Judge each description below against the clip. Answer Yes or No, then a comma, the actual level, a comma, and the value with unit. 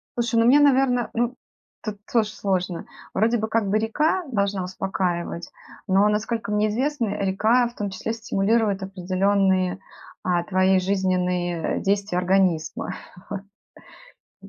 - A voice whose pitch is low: No, high, 200 Hz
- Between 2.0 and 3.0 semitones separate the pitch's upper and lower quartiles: No, average, 3.4 semitones